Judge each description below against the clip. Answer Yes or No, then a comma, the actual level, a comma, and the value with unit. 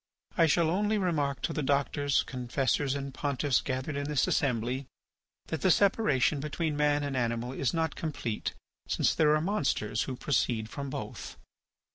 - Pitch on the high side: No, medium, 140 Hz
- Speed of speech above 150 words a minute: Yes, average, 160 wpm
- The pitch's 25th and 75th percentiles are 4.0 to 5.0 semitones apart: No, average, 2.9 semitones